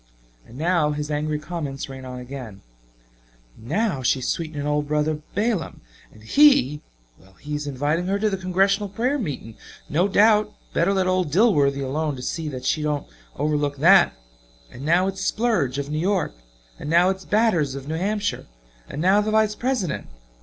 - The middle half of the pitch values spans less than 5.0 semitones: No, wide, 5.4 semitones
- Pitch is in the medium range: Yes, medium, 155 Hz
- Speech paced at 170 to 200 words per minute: Yes, average, 175 wpm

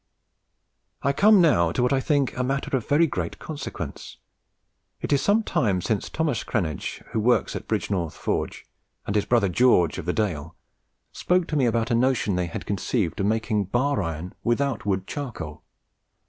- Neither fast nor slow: Yes, average, 175 wpm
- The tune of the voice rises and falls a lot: Yes, wide, 6.8 semitones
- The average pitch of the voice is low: Yes, low, 115 Hz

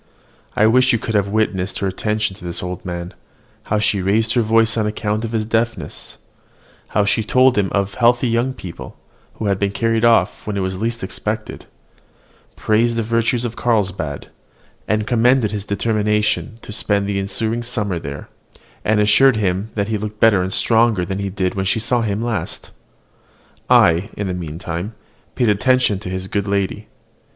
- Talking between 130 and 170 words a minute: No, average, 180 wpm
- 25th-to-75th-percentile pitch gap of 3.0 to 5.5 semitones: No, narrow, 2.6 semitones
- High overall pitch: No, low, 105 Hz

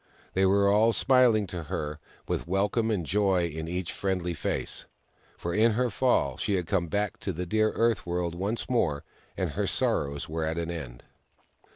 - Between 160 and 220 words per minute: Yes, average, 190 wpm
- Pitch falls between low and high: No, very low, 95 Hz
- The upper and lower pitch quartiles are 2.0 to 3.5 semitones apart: No, average, 4.2 semitones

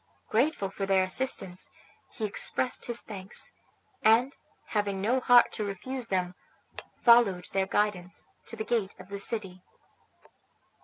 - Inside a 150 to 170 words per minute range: No, slow, 135 wpm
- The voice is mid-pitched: No, high, 205 Hz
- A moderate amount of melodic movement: Yes, average, 3.7 semitones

